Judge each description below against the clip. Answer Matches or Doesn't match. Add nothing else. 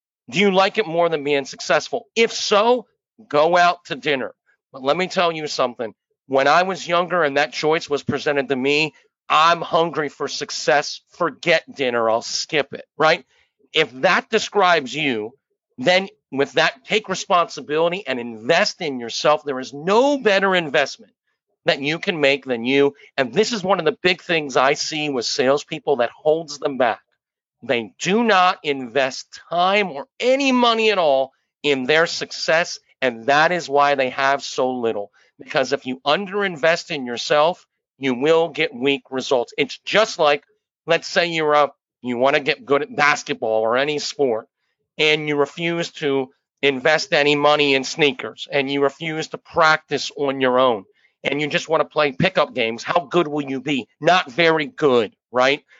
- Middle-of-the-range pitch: Matches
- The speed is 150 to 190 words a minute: Matches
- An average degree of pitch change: Matches